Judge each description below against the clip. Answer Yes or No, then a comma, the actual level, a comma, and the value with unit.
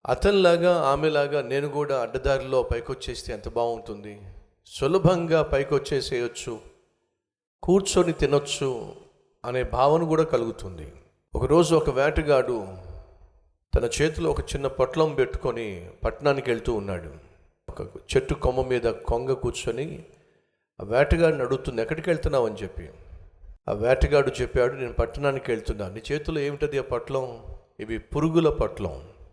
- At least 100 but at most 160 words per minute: Yes, average, 115 wpm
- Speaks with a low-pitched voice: Yes, low, 130 Hz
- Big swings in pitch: Yes, wide, 6.7 semitones